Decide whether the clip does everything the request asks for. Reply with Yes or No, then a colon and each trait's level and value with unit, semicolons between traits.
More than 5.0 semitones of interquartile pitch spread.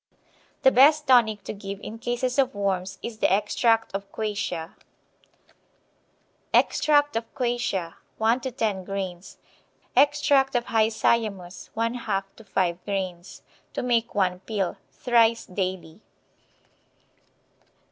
No: average, 3.9 semitones